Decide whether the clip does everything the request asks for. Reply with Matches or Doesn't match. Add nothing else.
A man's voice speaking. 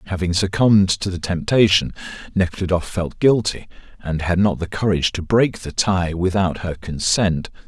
Matches